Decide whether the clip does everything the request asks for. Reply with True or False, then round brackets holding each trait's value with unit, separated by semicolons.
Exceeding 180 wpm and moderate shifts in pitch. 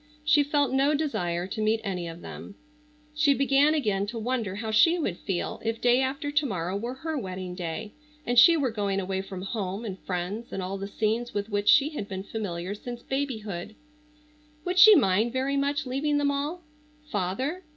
False (195 wpm; 6.3 semitones)